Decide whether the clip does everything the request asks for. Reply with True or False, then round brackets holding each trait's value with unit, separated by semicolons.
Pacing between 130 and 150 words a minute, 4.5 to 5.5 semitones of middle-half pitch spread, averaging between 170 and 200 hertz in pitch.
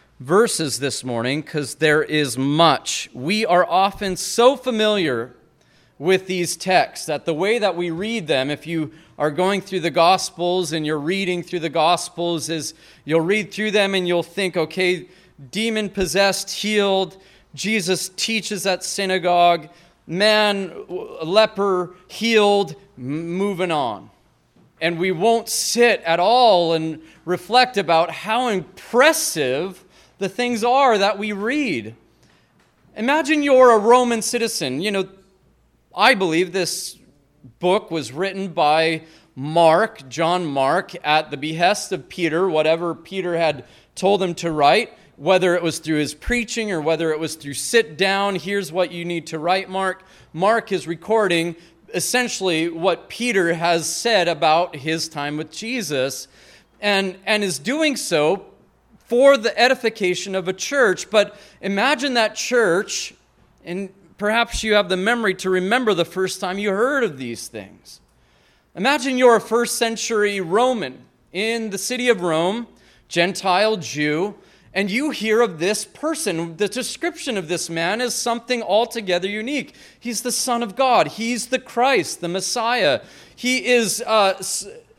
True (145 wpm; 4.9 semitones; 190 Hz)